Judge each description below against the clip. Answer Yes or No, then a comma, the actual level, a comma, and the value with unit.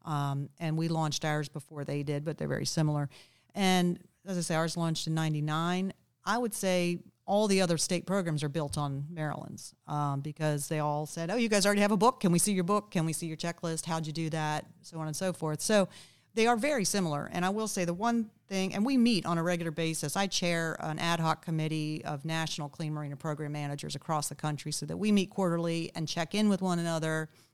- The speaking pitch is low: No, medium, 165 Hz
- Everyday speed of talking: No, fast, 235 wpm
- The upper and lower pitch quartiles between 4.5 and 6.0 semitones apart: No, average, 3.4 semitones